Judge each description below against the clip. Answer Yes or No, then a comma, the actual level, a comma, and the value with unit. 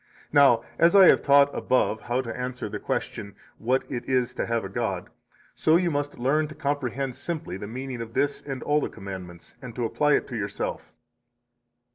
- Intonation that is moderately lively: Yes, average, 3.8 semitones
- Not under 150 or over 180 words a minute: No, average, 195 wpm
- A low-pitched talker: Yes, low, 130 Hz